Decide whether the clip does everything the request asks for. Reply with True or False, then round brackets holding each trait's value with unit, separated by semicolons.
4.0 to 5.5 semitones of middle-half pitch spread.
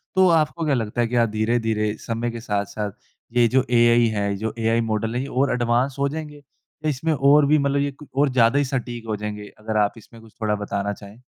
True (4.3 semitones)